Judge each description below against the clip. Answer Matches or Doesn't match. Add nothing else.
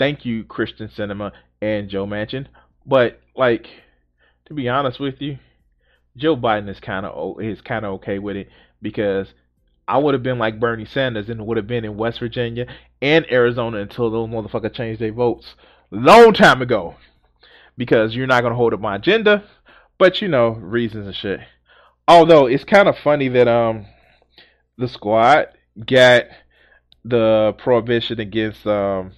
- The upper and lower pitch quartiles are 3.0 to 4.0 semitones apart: Matches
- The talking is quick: Doesn't match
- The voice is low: Matches